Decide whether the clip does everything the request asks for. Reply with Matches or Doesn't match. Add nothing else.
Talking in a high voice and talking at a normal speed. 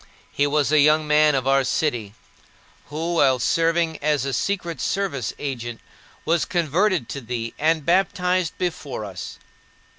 Doesn't match